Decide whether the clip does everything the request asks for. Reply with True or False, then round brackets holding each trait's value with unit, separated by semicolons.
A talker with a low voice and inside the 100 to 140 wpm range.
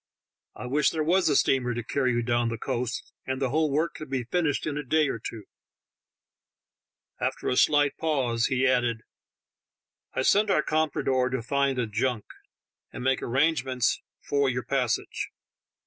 False (130 Hz; 170 wpm)